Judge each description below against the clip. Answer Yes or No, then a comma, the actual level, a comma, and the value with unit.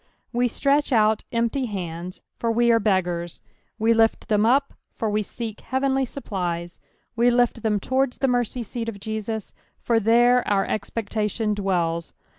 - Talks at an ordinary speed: Yes, average, 155 wpm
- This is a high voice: Yes, high, 225 Hz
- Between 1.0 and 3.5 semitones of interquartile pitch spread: Yes, average, 3.2 semitones